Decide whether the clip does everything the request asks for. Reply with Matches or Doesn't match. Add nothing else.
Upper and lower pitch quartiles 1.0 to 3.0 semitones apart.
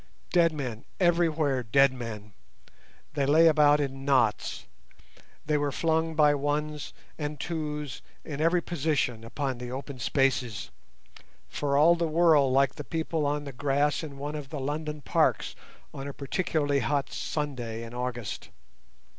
Matches